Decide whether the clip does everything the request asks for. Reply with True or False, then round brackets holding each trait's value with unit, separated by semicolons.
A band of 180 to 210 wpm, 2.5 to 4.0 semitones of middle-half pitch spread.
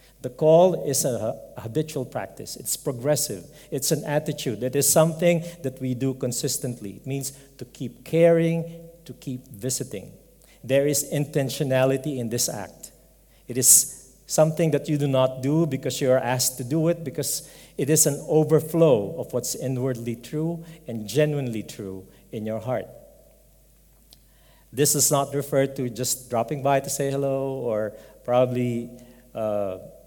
False (150 wpm; 3.2 semitones)